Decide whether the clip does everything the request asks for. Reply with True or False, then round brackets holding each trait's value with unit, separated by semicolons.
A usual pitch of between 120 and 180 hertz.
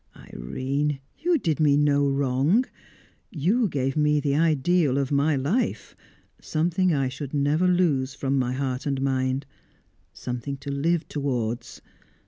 True (140 Hz)